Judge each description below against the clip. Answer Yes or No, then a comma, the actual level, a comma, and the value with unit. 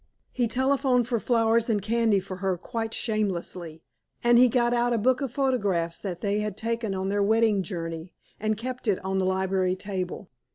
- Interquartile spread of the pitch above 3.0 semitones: Yes, average, 4.0 semitones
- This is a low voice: No, high, 215 Hz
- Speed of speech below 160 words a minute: No, average, 190 wpm